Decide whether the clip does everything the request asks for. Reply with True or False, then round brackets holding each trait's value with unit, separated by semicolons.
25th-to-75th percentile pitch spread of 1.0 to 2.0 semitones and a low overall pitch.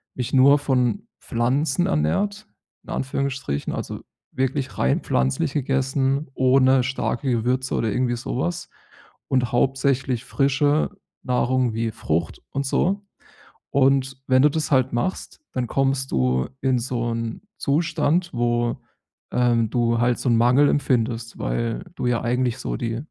False (2.6 semitones; 130 Hz)